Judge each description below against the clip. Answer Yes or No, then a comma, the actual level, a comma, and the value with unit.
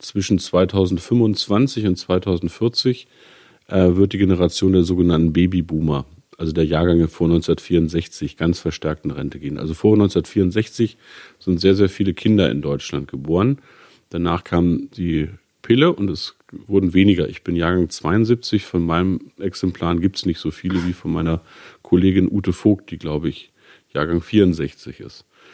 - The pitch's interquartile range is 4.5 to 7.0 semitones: No, average, 2.9 semitones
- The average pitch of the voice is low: Yes, very low, 90 Hz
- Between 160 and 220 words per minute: No, average, 150 wpm